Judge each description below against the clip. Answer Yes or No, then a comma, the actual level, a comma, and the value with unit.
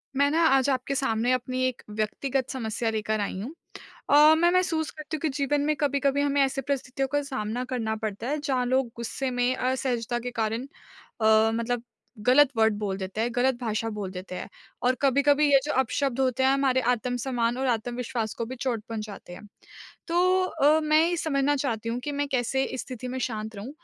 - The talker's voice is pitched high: Yes, very high, 255 Hz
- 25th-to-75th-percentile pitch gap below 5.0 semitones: Yes, average, 3.6 semitones